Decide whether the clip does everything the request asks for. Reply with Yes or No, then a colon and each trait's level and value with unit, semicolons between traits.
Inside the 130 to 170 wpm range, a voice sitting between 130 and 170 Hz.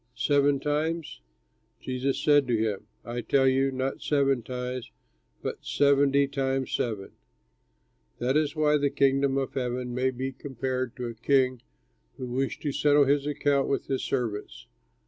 Yes: average, 150 wpm; low, 135 Hz